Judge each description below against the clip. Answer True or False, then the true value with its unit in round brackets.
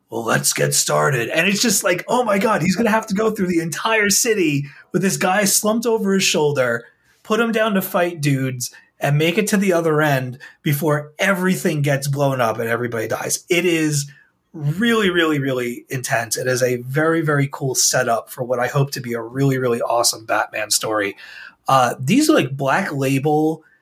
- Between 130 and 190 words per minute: False (200 wpm)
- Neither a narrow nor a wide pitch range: False (6.4 semitones)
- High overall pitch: False (155 Hz)